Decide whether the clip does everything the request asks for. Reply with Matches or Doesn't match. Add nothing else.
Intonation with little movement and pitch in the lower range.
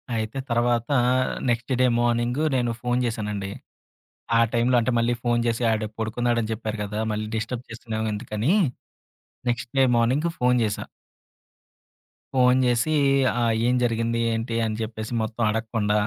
Matches